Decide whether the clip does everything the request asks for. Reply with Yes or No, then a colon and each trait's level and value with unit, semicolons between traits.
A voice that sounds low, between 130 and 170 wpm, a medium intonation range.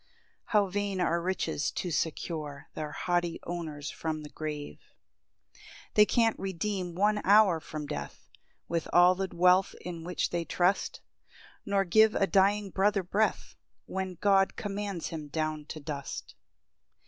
No: medium, 180 Hz; average, 145 wpm; average, 3.7 semitones